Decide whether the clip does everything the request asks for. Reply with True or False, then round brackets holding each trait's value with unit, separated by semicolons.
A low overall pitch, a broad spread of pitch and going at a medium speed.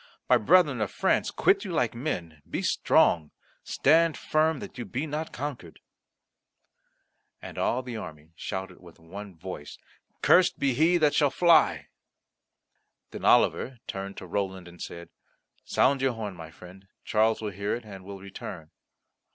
True (105 Hz; 7.3 semitones; 155 wpm)